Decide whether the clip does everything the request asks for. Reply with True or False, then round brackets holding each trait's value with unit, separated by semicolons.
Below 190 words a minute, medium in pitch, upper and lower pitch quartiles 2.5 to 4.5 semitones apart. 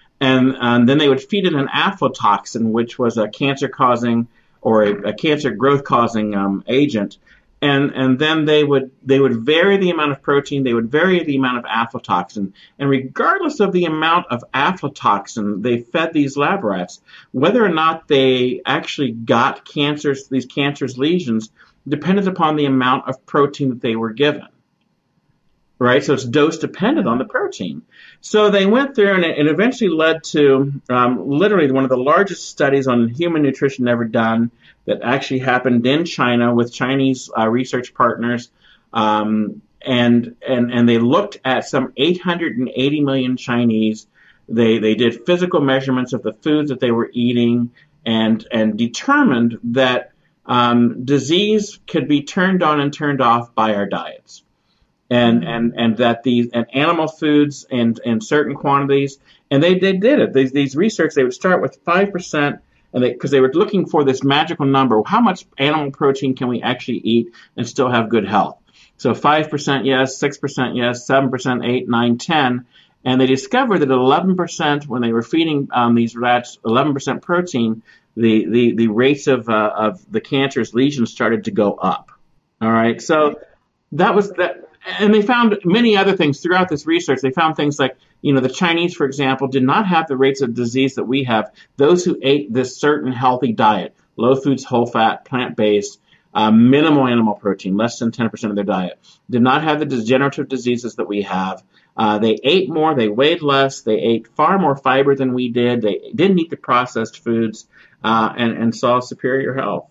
False (180 wpm; 130 Hz; 4.1 semitones)